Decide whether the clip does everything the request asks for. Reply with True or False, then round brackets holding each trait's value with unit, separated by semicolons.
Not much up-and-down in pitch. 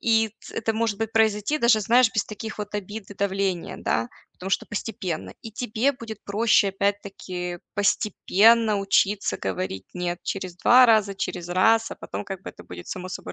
False (3.1 semitones)